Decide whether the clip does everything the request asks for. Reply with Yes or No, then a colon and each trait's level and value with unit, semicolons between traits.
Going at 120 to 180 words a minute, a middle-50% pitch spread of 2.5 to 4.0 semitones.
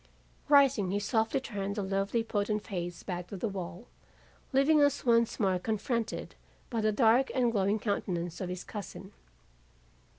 Yes: average, 155 wpm; average, 3.4 semitones